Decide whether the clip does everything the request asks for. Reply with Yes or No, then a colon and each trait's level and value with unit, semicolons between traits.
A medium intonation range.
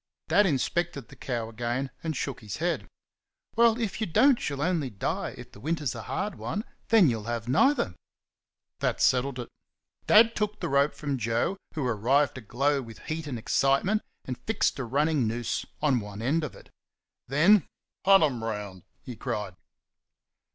No: wide, 6.2 semitones